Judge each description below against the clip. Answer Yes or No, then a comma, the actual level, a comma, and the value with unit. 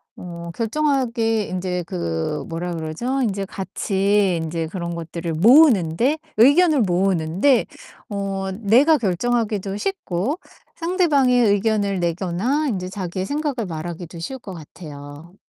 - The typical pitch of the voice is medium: No, high, 195 Hz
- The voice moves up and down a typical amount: No, wide, 6.0 semitones